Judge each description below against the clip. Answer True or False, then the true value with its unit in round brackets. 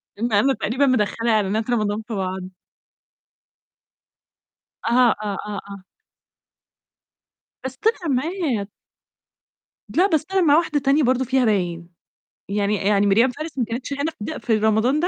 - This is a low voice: False (235 Hz)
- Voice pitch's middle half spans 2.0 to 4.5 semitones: False (5.1 semitones)